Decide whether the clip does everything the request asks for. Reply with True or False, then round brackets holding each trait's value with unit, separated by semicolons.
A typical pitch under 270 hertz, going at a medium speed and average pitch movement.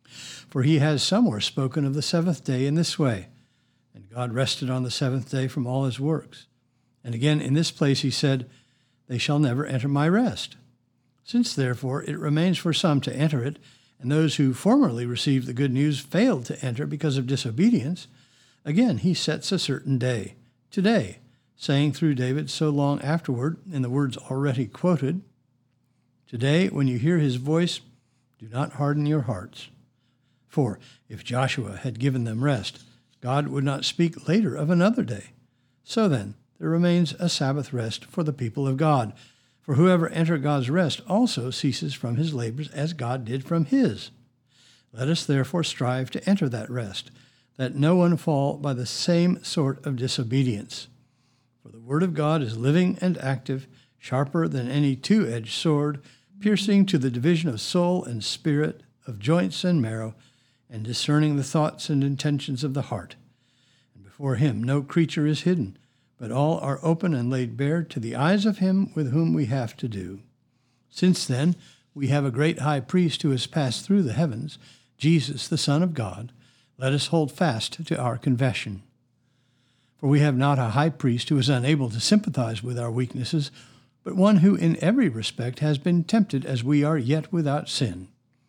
True (135 Hz; 180 wpm; 3.9 semitones)